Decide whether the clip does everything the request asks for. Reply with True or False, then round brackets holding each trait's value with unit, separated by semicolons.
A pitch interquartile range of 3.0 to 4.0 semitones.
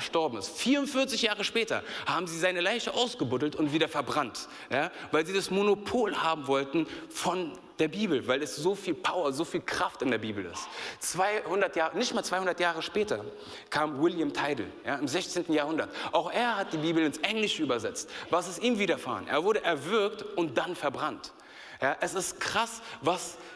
False (4.9 semitones)